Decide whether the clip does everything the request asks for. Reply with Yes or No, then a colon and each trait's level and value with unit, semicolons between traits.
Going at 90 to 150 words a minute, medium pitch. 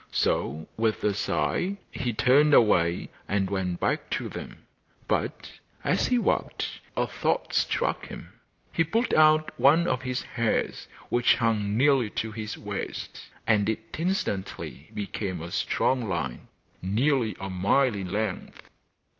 No: average, 140 wpm; low, 110 Hz